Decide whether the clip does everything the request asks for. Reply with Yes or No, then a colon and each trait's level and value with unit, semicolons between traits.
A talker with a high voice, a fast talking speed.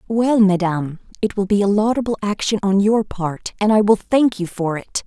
Yes: high, 205 Hz; fast, 215 wpm